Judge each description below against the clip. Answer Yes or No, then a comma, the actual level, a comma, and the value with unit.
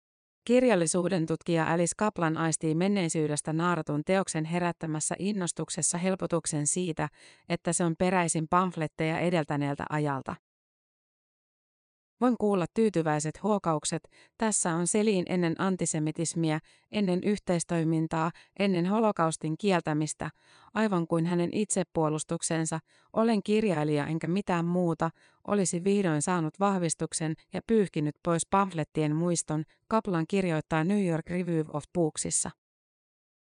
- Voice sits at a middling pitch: Yes, medium, 170 Hz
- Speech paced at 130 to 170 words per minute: No, average, 105 wpm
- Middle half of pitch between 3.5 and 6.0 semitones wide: No, average, 2.8 semitones